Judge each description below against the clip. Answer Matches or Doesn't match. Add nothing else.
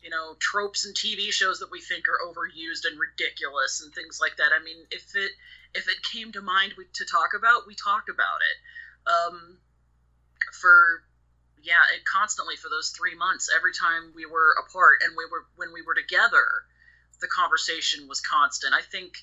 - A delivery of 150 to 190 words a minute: Matches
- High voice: Matches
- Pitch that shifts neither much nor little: Doesn't match